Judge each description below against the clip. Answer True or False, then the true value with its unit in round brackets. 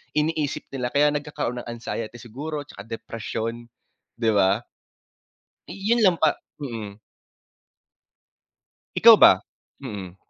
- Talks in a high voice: False (120 Hz)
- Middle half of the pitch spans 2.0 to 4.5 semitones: False (5.2 semitones)